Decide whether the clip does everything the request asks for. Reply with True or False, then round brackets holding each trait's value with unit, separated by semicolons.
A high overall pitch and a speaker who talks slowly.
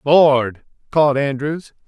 False (140 Hz; 95 wpm)